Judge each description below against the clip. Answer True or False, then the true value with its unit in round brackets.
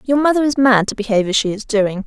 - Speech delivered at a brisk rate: True (290 wpm)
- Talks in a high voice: True (230 Hz)